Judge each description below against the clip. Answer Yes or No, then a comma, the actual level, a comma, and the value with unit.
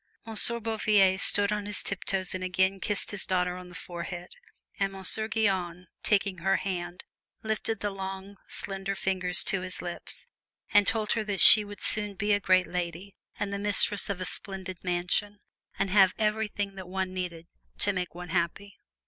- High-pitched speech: Yes, high, 195 Hz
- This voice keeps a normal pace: Yes, average, 175 wpm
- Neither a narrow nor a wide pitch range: No, narrow, 2.1 semitones